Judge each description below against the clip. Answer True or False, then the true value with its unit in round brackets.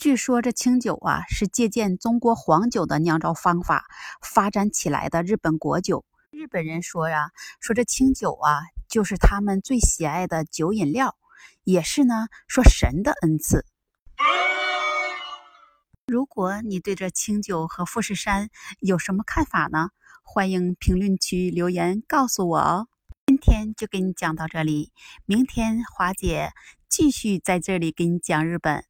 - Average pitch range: True (5.0 semitones)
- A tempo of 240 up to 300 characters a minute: False (225 characters per minute)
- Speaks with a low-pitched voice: False (190 Hz)